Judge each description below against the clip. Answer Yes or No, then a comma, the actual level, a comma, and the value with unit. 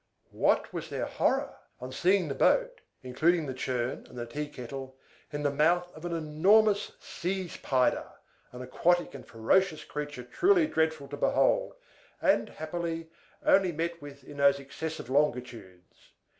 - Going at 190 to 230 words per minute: No, average, 150 wpm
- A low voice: No, medium, 150 Hz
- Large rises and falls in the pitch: No, average, 4.9 semitones